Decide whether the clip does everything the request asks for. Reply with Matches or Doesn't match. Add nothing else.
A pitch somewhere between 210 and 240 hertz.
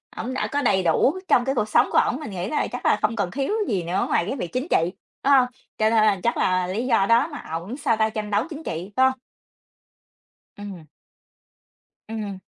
Matches